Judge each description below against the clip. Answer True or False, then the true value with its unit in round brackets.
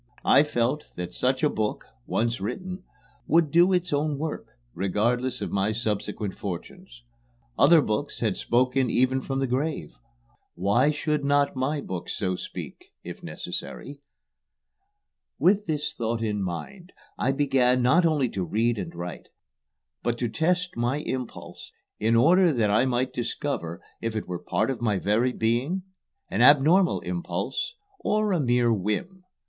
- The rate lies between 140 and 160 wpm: True (155 wpm)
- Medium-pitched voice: False (130 Hz)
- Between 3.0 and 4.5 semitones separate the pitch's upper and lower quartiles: False (5.5 semitones)